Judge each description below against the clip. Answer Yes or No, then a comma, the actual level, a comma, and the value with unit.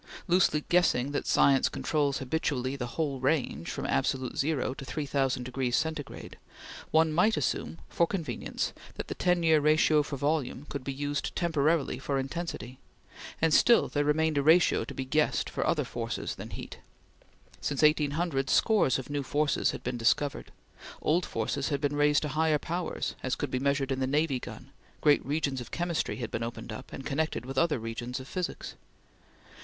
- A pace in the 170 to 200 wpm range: Yes, average, 180 wpm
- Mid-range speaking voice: Yes, medium, 145 Hz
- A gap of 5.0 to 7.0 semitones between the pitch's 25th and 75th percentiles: No, average, 3.2 semitones